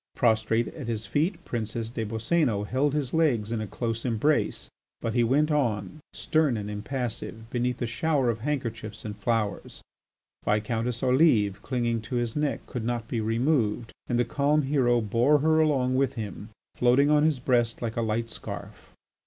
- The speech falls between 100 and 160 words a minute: No, average, 170 wpm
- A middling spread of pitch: Yes, average, 3.8 semitones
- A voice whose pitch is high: No, low, 120 Hz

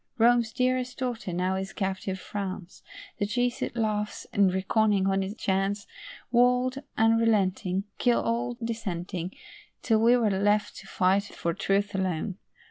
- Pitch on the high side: Yes, high, 205 Hz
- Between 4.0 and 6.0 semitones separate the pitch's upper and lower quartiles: No, average, 3.5 semitones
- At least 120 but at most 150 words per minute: Yes, slow, 135 wpm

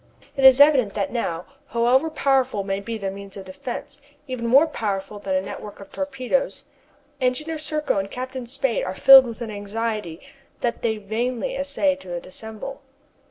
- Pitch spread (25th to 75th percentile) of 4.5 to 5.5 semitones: Yes, average, 5.2 semitones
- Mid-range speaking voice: No, high, 235 Hz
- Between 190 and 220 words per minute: No, average, 165 wpm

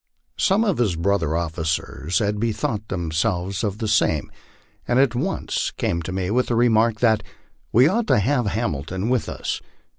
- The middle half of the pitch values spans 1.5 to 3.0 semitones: No, average, 5.3 semitones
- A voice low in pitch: Yes, low, 105 Hz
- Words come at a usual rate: Yes, average, 180 wpm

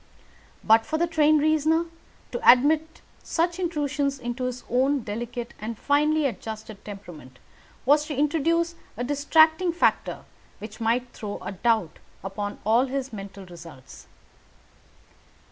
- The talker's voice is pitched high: Yes, very high, 255 Hz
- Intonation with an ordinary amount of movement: No, wide, 6.1 semitones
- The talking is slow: Yes, slow, 130 wpm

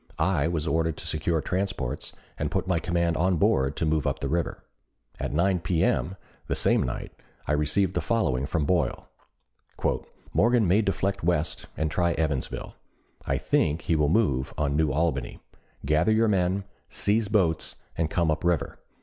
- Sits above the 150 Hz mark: No, very low, 85 Hz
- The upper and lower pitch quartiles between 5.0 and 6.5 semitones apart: No, average, 3.5 semitones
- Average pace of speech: Yes, average, 165 wpm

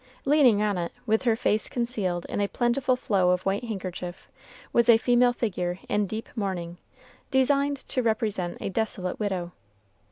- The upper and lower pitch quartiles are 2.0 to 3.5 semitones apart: No, average, 4.7 semitones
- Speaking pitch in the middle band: No, high, 215 Hz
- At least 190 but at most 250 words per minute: No, average, 160 wpm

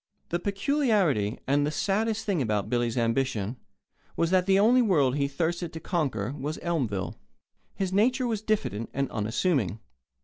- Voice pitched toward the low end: No, medium, 160 Hz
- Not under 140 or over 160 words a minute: Yes, average, 150 wpm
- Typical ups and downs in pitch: No, wide, 8.4 semitones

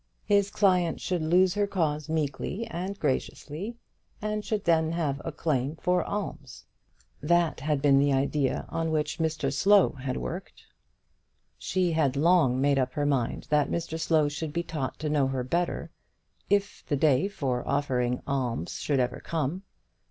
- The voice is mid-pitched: Yes, medium, 155 Hz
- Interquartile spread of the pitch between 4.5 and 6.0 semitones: No, average, 4.1 semitones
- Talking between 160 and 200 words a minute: Yes, average, 165 wpm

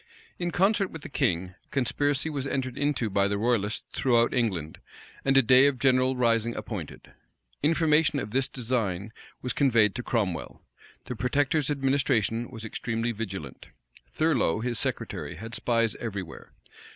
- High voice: No, low, 120 Hz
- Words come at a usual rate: Yes, average, 150 wpm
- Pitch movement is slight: No, average, 4.2 semitones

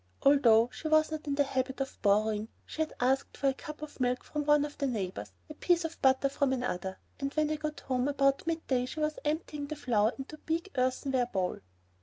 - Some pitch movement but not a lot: Yes, average, 3.5 semitones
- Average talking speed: No, fast, 225 wpm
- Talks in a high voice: Yes, very high, 275 Hz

